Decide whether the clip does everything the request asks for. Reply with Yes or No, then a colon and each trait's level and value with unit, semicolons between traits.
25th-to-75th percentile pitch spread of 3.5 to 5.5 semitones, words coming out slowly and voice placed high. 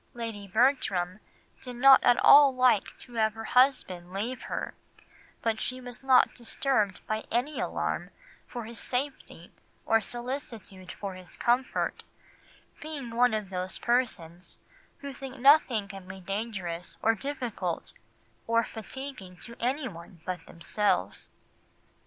Yes: average, 4.8 semitones; slow, 130 wpm; high, 230 Hz